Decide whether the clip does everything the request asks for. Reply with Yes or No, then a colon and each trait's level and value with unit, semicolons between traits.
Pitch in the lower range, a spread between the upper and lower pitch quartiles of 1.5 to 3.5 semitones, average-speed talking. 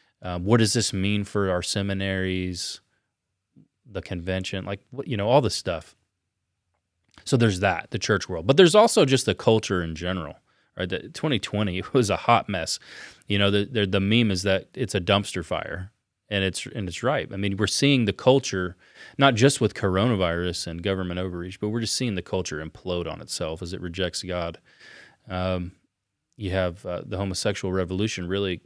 Yes: very low, 95 Hz; average, 2.8 semitones; average, 185 wpm